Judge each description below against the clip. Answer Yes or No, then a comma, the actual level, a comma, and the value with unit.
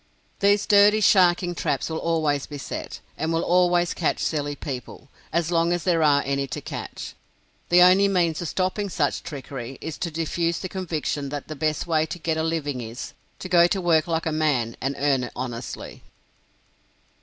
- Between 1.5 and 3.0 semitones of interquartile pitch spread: No, average, 3.5 semitones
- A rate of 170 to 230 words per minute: Yes, average, 190 wpm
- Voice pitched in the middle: Yes, medium, 160 Hz